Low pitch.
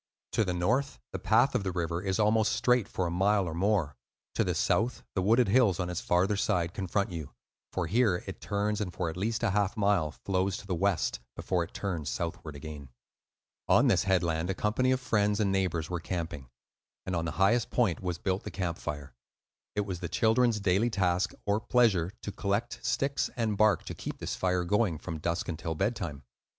Yes: very low, 95 Hz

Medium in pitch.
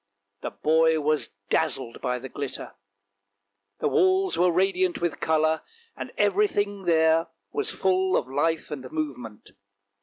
Yes: medium, 160 Hz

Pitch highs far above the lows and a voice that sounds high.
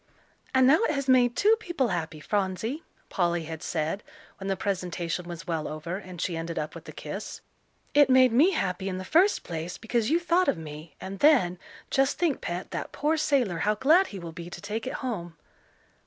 Yes: wide, 7.8 semitones; high, 195 Hz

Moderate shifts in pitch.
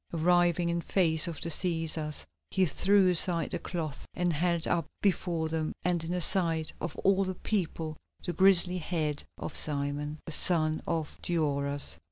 No: narrow, 2.3 semitones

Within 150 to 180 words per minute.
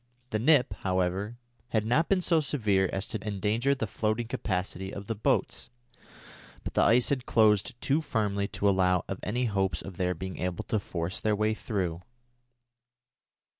Yes: average, 170 wpm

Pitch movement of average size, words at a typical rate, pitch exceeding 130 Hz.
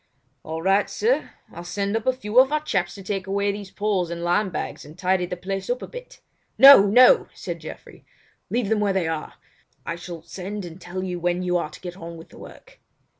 No: average, 3.1 semitones; fast, 225 wpm; high, 190 Hz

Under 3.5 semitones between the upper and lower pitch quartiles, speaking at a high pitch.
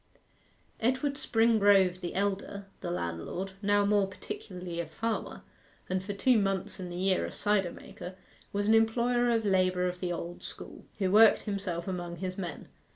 Yes: average, 2.7 semitones; high, 195 Hz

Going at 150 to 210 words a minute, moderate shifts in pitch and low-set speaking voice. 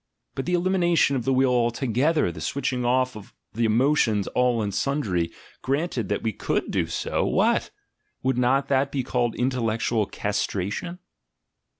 Yes: average, 155 wpm; average, 3.8 semitones; low, 125 Hz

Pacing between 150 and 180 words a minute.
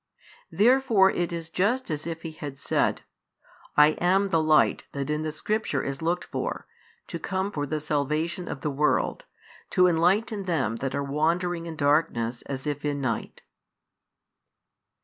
Yes: average, 160 wpm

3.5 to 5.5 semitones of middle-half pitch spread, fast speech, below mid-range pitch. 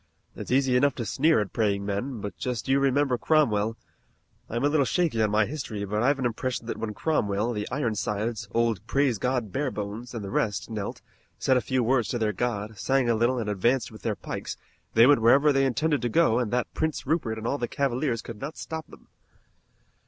Yes: average, 3.9 semitones; fast, 210 wpm; low, 120 Hz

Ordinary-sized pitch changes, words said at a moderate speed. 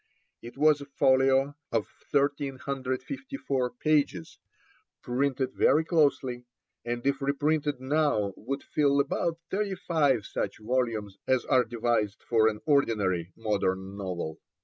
No: average, 4.2 semitones; slow, 120 wpm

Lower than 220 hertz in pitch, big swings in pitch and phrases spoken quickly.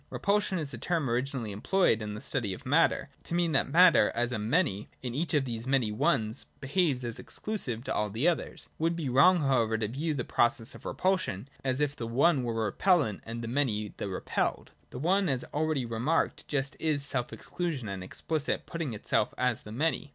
Yes: low, 135 Hz; wide, 5.9 semitones; fast, 210 wpm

